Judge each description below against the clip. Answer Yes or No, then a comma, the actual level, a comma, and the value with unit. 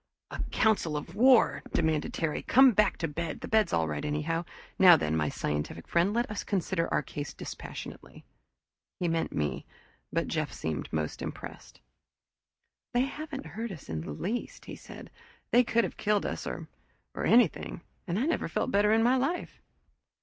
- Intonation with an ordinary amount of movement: No, wide, 7.4 semitones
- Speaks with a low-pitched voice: No, medium, 175 Hz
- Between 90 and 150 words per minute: No, average, 180 wpm